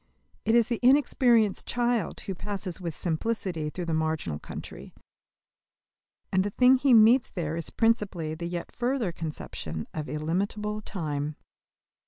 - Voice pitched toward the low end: No, high, 190 Hz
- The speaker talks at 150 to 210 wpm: No, average, 140 wpm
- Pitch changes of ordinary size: No, wide, 6.4 semitones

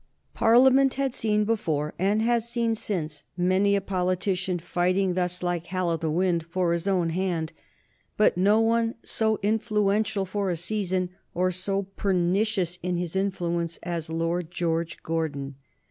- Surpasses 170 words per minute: No, average, 150 wpm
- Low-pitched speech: No, medium, 185 Hz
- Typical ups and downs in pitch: Yes, average, 3.5 semitones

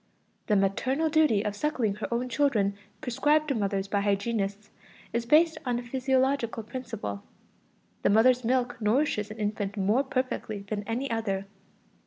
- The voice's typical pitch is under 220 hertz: No, high, 230 Hz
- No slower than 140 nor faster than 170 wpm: Yes, average, 150 wpm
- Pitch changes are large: No, average, 4.2 semitones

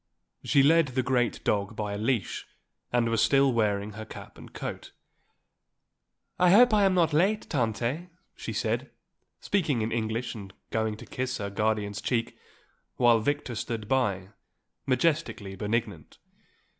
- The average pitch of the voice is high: No, low, 115 Hz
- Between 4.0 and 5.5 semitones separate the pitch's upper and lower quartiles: Yes, average, 4.5 semitones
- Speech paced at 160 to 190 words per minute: No, average, 145 wpm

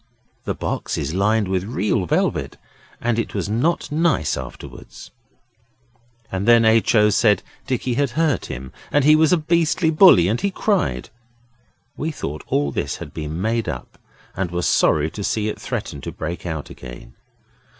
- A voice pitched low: Yes, low, 105 Hz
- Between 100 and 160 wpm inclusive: No, average, 170 wpm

